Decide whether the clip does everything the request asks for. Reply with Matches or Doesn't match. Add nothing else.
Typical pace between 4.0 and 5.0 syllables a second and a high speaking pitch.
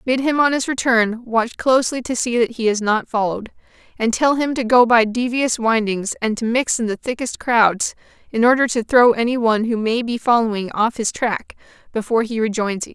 Doesn't match